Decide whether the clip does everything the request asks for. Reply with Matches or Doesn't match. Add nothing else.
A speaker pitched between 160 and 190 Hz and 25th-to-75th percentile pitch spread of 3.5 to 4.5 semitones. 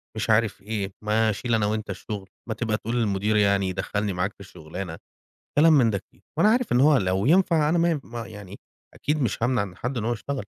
Doesn't match